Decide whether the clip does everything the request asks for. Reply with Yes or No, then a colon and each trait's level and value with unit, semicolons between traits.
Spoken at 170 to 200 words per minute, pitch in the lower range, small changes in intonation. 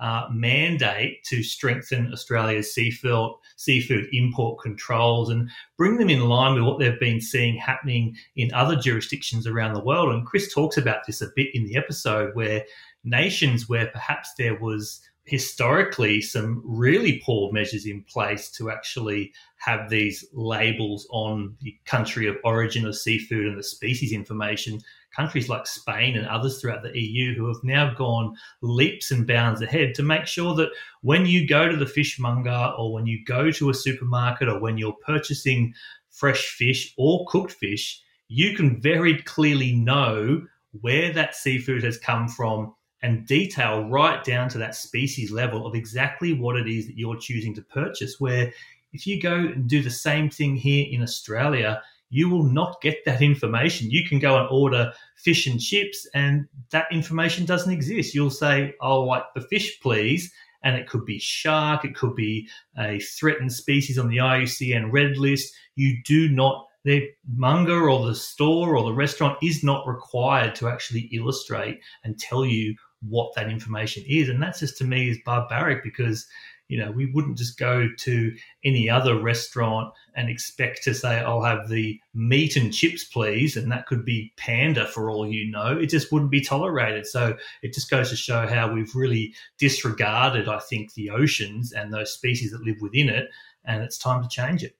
No: average, 180 wpm; low, 125 Hz; average, 3.8 semitones